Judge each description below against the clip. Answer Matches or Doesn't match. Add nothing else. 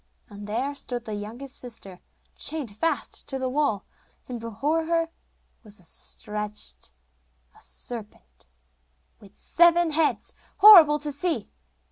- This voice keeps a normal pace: Doesn't match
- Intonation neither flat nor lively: Doesn't match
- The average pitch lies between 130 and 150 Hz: Doesn't match